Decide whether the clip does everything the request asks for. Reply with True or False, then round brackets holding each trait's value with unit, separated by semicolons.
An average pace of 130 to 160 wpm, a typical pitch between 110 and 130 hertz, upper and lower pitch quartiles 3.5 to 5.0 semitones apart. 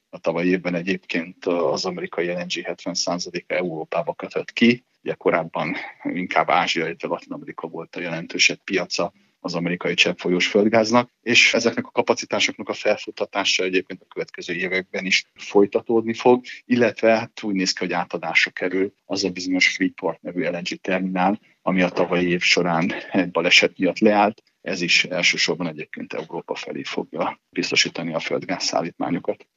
False (155 wpm; 95 Hz; 3.9 semitones)